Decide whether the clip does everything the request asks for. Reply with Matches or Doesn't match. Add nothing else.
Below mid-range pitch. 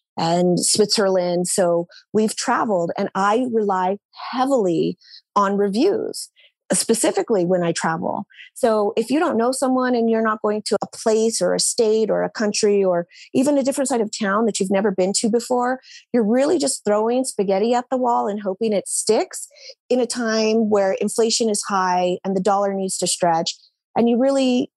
Doesn't match